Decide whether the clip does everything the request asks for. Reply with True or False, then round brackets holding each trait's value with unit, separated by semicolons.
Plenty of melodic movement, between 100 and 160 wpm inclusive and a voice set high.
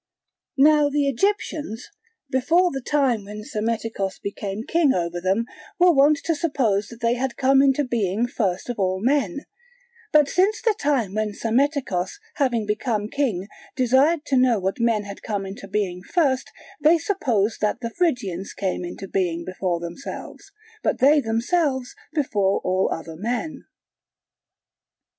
True (6.2 semitones; 150 wpm; 235 Hz)